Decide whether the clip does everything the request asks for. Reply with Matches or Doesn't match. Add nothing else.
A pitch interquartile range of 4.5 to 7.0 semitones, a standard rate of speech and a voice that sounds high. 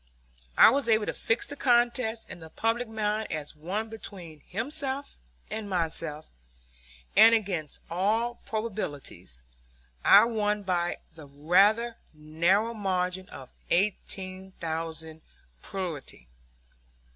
Doesn't match